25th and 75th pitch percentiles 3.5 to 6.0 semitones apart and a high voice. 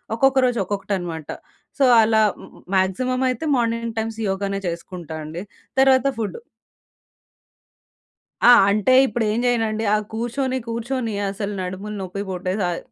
Yes: average, 4.0 semitones; high, 220 Hz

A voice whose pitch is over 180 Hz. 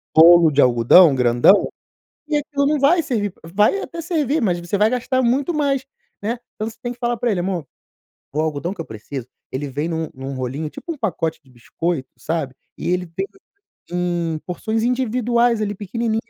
Yes: high, 190 Hz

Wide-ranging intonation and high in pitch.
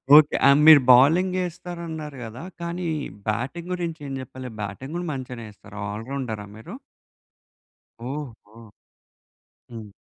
No: wide, 6.5 semitones; low, 135 Hz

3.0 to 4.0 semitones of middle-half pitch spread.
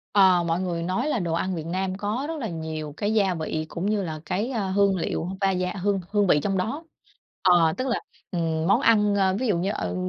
Yes: average, 3.6 semitones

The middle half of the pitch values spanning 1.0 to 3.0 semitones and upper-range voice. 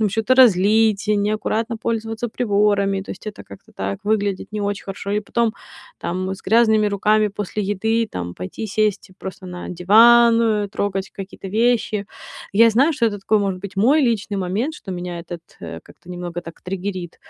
Yes: average, 2.7 semitones; high, 205 Hz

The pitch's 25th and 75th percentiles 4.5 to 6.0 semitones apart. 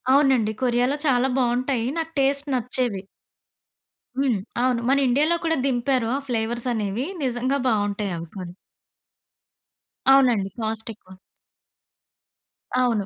No: average, 3.3 semitones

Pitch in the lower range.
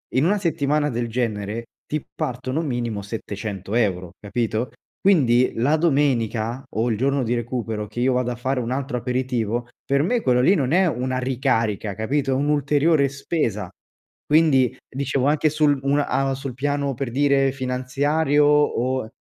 Yes: low, 130 Hz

